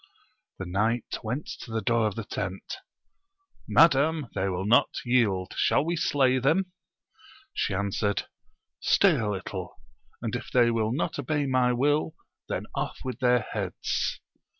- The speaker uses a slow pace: No, average, 150 wpm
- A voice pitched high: No, low, 120 Hz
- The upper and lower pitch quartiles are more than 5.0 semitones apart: Yes, wide, 5.6 semitones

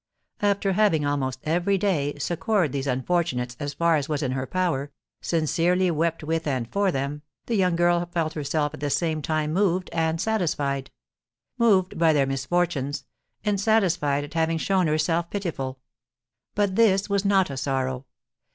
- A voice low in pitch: No, medium, 165 Hz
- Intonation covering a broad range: No, average, 4.4 semitones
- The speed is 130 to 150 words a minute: No, average, 160 wpm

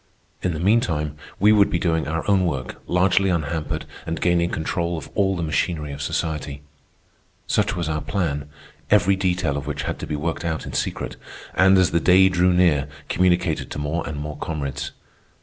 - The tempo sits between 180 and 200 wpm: Yes, average, 185 wpm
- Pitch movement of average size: Yes, average, 3.3 semitones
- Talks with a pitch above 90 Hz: No, very low, 85 Hz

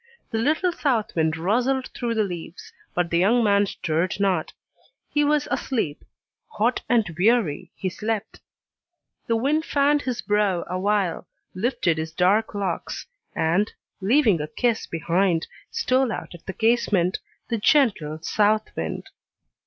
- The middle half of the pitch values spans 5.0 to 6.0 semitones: Yes, wide, 5.4 semitones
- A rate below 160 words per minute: Yes, average, 140 wpm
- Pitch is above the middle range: Yes, high, 210 Hz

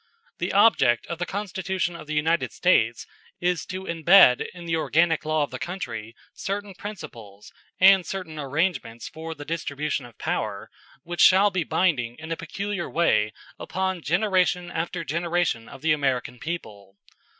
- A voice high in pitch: No, medium, 165 Hz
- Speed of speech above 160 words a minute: No, average, 155 wpm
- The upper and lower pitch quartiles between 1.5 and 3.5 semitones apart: No, average, 4.7 semitones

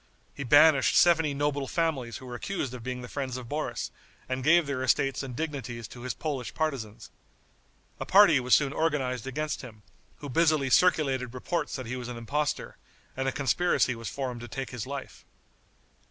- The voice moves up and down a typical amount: Yes, average, 3.3 semitones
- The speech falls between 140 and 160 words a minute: No, average, 185 wpm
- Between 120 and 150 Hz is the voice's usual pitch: Yes, low, 135 Hz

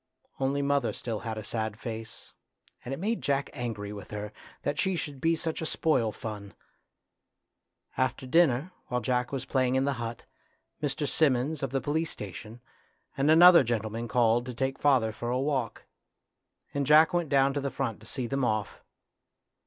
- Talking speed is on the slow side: No, average, 175 wpm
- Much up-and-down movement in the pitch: No, average, 3.8 semitones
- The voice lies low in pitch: Yes, low, 130 Hz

